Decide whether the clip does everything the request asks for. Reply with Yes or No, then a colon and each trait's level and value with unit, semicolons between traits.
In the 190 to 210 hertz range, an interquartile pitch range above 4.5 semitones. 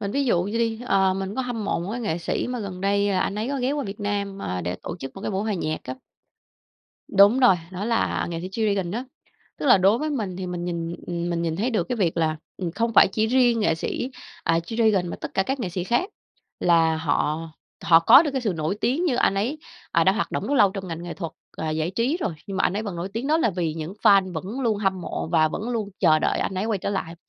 Yes: high, 195 Hz; average, 4.9 semitones